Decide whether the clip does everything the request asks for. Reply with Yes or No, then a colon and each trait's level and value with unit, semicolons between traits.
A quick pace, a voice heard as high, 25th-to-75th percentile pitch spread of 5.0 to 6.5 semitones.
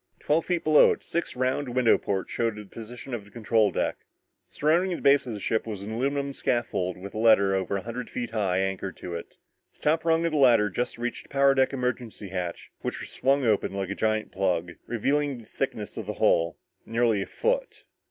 No: fast, 220 wpm; low, 115 Hz; wide, 5.5 semitones